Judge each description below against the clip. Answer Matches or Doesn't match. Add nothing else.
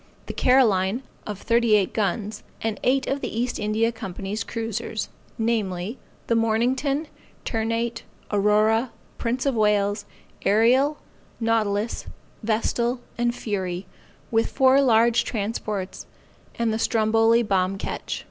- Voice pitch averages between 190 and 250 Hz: Matches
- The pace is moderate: Doesn't match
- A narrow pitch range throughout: Matches